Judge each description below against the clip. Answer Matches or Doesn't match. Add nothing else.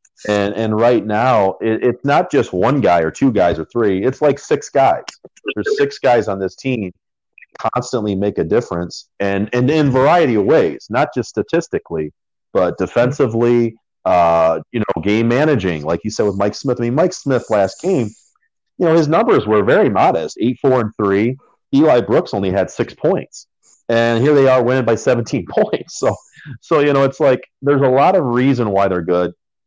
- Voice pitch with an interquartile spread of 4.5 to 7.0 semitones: Matches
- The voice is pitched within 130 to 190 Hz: Doesn't match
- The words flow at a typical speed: Matches